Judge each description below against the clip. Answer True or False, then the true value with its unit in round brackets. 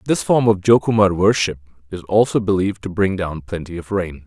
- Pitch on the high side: False (95 Hz)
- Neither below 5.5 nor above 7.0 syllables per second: True (5.9 syllables/s)